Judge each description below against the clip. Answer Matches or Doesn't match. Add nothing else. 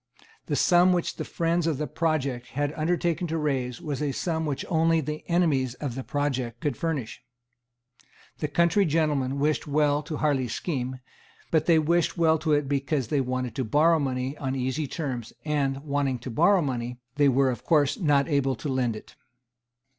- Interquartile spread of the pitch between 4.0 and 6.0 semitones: Doesn't match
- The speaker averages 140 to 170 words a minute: Doesn't match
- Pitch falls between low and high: Matches